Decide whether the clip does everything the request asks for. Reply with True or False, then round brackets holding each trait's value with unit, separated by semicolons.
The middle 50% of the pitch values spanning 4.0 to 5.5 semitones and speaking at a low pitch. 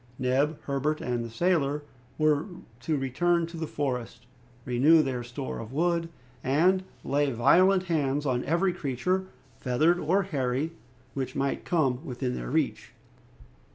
False (4.7 semitones; 145 Hz)